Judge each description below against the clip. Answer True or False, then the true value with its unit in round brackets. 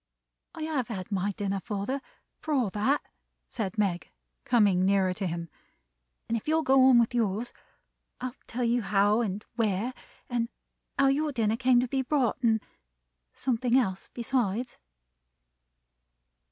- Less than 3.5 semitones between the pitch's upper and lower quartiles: False (4.3 semitones)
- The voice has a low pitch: False (230 Hz)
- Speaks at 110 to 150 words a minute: True (145 wpm)